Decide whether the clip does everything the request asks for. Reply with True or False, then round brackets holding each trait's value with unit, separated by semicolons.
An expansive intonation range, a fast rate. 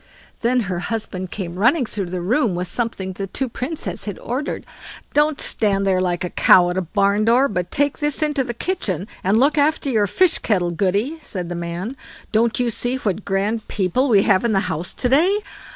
True (5.7 semitones; 210 wpm)